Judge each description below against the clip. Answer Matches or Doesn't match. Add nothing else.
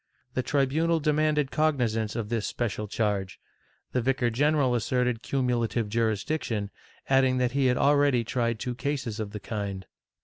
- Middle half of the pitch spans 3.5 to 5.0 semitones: Matches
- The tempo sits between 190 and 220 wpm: Doesn't match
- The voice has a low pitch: Matches